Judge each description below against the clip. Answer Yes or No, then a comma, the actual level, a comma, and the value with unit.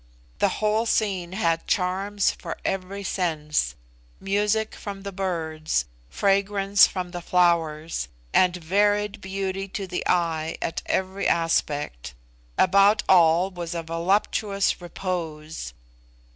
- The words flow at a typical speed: No, slow, 115 wpm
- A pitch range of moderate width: Yes, average, 3.1 semitones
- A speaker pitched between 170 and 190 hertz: Yes, medium, 185 Hz